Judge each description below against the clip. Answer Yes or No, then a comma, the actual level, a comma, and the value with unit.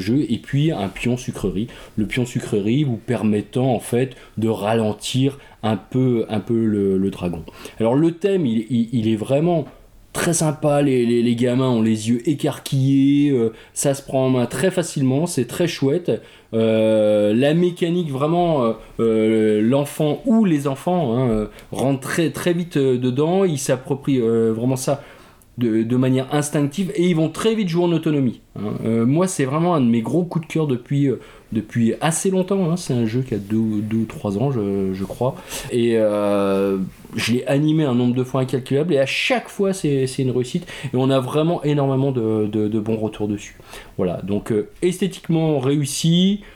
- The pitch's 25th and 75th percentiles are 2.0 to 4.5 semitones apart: No, average, 5.3 semitones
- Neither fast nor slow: Yes, average, 195 wpm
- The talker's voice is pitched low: Yes, low, 130 Hz